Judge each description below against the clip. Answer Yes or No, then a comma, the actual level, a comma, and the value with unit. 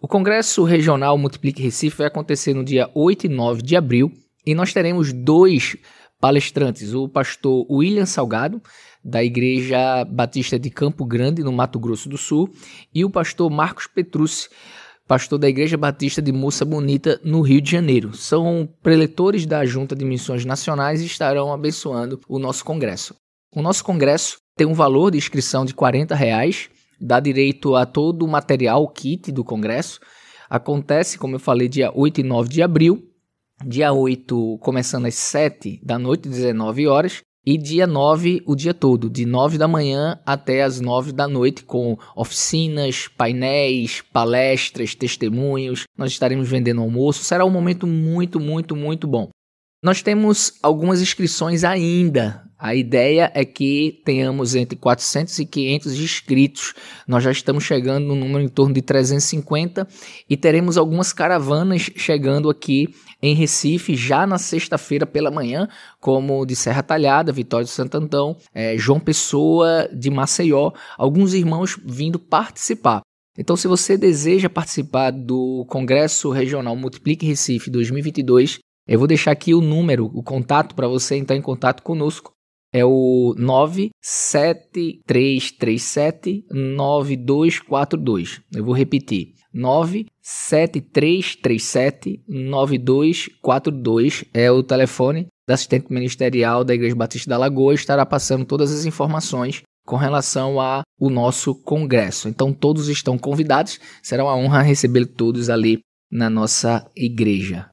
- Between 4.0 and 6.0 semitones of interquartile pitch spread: No, average, 3.5 semitones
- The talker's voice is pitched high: No, medium, 140 Hz